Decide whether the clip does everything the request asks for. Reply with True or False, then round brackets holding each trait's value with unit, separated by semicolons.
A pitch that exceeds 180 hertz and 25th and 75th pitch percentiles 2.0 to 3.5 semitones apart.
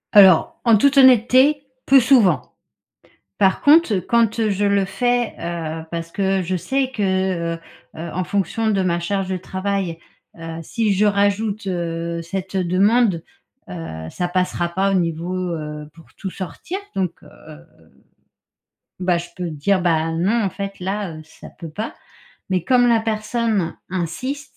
False (190 Hz; 4.2 semitones)